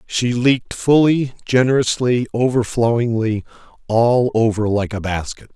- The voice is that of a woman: No, male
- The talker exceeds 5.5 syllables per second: No, 4.4 syllables/s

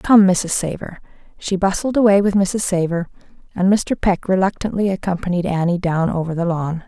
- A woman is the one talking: Yes, female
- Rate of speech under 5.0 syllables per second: No, 5.2 syllables/s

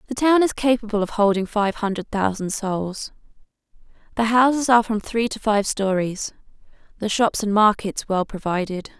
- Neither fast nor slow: Yes, average, 160 wpm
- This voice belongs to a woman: Yes, female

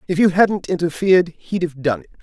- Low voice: No, medium, 170 Hz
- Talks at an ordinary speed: No, fast, 215 wpm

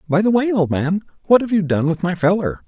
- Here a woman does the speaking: No, male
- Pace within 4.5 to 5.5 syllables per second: No, 5.9 syllables/s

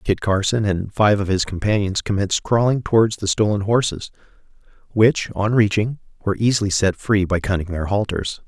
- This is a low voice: Yes, low, 100 Hz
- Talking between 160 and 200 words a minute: Yes, average, 170 wpm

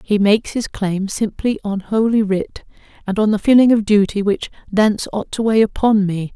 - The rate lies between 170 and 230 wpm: Yes, average, 200 wpm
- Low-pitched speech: No, high, 210 Hz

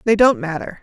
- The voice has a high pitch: Yes, high, 205 Hz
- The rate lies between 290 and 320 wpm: No, fast, 220 wpm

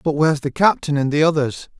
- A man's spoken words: Yes, male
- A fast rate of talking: Yes, fast, 235 wpm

